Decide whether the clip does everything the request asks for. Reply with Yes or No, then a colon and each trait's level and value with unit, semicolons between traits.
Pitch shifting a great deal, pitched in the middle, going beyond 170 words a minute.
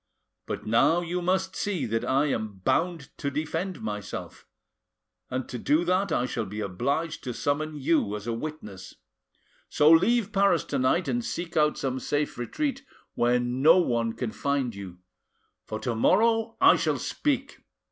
No: wide, 7.1 semitones; medium, 150 Hz; average, 160 wpm